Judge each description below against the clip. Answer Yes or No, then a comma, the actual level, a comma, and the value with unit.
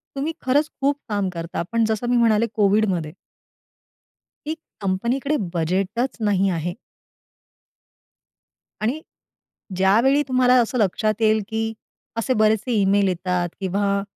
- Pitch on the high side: Yes, high, 215 Hz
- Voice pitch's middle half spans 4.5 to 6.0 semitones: No, average, 4.1 semitones